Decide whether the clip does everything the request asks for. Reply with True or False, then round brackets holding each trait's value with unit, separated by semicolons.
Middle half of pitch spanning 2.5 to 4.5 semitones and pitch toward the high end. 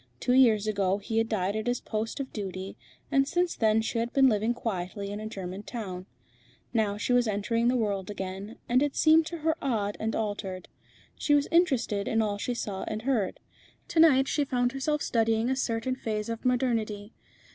True (3.9 semitones; 225 Hz)